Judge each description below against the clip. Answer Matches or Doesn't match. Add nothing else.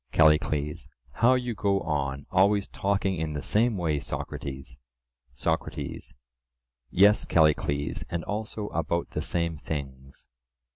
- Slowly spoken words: Matches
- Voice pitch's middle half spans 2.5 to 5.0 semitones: Doesn't match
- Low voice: Matches